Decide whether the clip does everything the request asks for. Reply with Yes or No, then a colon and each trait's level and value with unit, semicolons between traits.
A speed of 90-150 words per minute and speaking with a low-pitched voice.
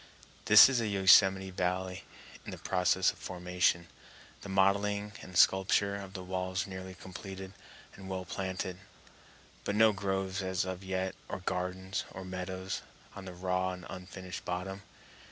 Yes: average, 140 wpm; very low, 95 Hz